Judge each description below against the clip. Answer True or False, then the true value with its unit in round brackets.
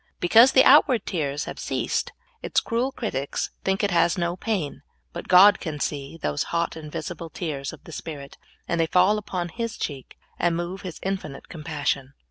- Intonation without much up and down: False (4.6 semitones)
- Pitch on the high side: False (170 Hz)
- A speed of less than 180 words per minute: False (185 wpm)